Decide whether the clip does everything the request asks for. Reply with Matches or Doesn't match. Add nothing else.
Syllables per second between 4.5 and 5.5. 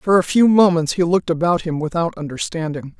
Doesn't match